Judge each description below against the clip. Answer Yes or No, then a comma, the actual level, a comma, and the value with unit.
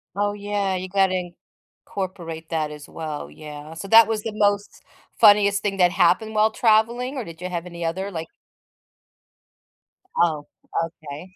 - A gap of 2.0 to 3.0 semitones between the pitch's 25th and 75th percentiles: No, average, 3.9 semitones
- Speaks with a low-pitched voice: No, medium, 185 Hz